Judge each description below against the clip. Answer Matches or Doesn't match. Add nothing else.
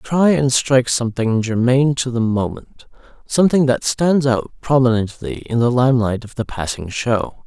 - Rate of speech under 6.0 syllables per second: Matches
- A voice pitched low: Matches